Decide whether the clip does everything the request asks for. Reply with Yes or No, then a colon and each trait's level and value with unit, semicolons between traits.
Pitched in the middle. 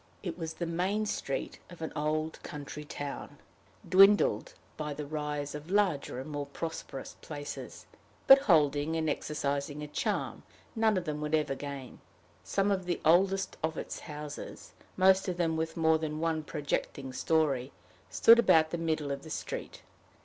Yes: medium, 155 Hz